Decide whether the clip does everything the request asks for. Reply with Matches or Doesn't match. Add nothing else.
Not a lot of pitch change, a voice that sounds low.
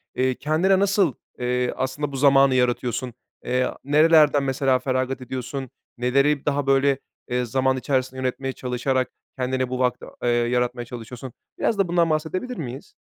Matches